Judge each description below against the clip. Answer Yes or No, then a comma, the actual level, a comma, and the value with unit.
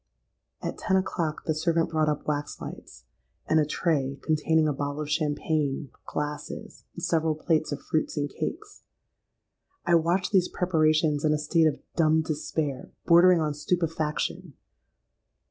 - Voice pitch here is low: No, medium, 155 Hz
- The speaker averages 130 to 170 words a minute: Yes, average, 145 wpm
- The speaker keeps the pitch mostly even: Yes, narrow, 2.0 semitones